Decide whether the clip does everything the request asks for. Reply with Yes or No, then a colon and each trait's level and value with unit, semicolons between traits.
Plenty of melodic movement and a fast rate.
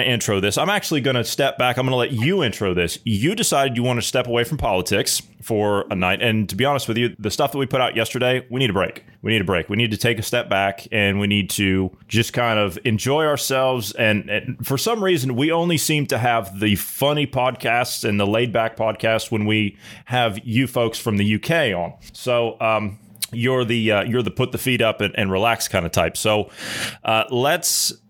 No: average, 3.4 semitones; fast, 235 wpm